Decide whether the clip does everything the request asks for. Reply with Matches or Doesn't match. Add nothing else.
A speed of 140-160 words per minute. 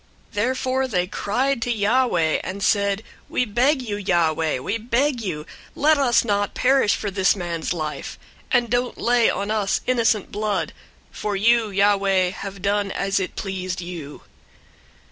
Matches